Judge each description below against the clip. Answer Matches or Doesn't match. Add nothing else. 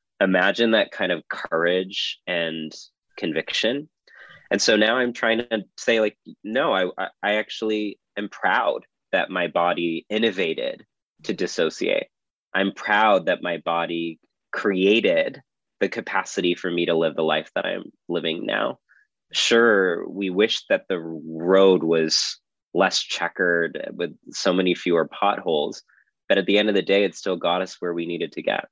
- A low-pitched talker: Matches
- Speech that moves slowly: Doesn't match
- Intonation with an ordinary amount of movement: Matches